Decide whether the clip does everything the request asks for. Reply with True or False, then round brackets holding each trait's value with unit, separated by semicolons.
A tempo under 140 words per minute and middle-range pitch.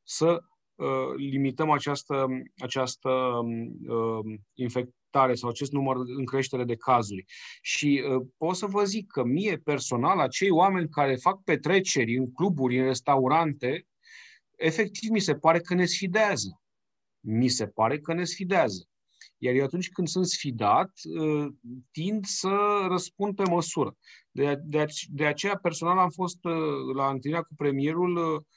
False (145 wpm; 150 Hz)